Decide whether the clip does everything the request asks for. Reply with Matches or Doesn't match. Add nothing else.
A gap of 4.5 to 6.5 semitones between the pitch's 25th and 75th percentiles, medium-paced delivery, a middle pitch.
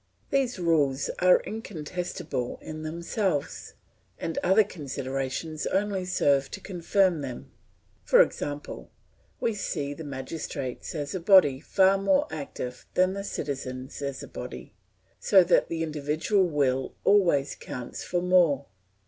Doesn't match